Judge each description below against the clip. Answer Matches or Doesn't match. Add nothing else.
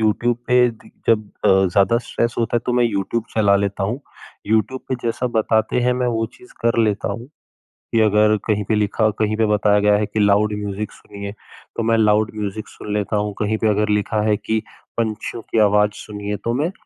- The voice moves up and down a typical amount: Doesn't match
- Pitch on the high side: Doesn't match